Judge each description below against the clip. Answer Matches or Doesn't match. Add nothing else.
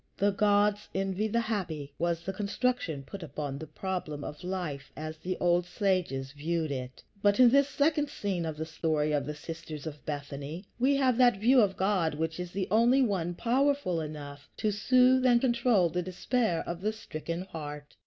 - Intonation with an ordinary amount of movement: Doesn't match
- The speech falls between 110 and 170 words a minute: Doesn't match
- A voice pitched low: Doesn't match